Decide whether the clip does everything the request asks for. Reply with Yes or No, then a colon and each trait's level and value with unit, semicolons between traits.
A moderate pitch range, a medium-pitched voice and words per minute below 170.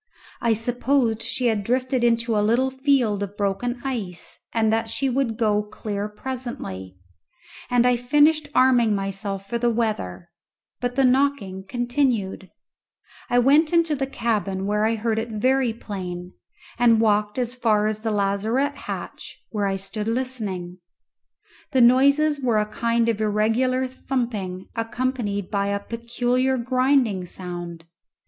No: average, 3.7 semitones; high, 230 Hz; average, 145 wpm